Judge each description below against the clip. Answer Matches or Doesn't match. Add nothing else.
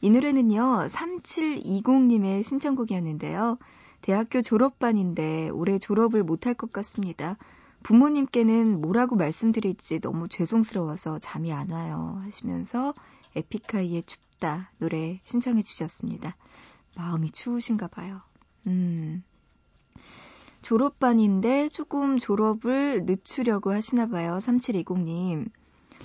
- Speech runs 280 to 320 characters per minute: Doesn't match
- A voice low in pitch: Doesn't match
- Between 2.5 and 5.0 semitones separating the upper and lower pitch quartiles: Doesn't match